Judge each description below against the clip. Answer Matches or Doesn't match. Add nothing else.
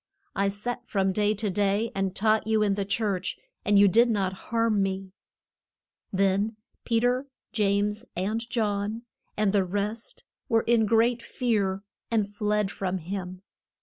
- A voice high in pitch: Matches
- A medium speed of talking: Matches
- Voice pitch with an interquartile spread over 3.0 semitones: Doesn't match